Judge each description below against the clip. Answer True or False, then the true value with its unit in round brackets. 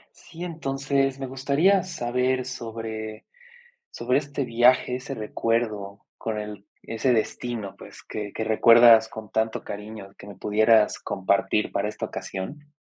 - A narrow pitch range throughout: False (3.6 semitones)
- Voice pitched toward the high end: False (115 Hz)